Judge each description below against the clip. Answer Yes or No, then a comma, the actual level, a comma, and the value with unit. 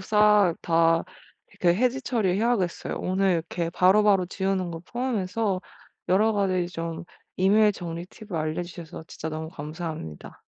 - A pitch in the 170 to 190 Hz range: Yes, medium, 185 Hz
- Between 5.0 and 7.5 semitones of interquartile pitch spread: No, average, 3.8 semitones